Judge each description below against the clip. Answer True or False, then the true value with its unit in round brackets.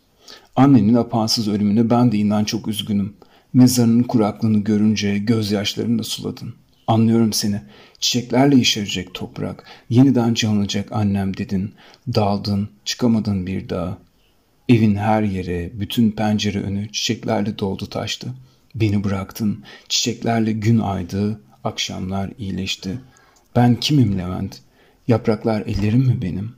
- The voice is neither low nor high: False (105 Hz)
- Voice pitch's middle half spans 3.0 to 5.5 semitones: False (2.6 semitones)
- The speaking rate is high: False (115 wpm)